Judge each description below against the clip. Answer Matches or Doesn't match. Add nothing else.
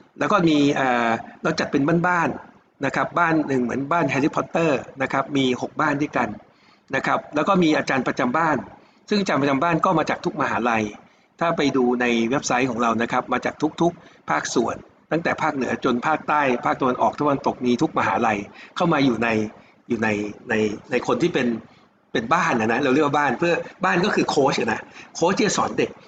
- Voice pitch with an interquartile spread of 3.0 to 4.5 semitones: Doesn't match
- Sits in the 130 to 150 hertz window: Matches